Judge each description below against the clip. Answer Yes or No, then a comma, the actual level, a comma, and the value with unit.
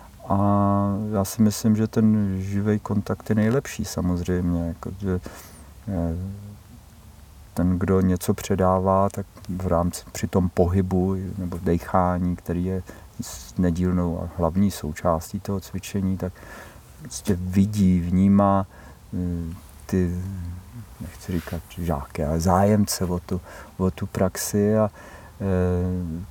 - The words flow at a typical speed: No, slow, 110 wpm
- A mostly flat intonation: Yes, narrow, 2.3 semitones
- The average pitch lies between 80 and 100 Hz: Yes, very low, 95 Hz